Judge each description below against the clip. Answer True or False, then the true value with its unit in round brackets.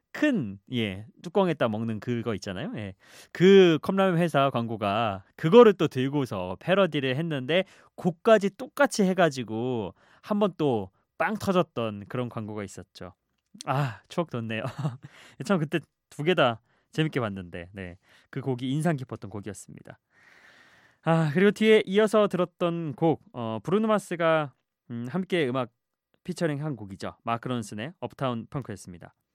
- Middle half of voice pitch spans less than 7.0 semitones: False (8.0 semitones)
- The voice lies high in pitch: False (135 Hz)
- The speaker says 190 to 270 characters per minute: False (290 characters per minute)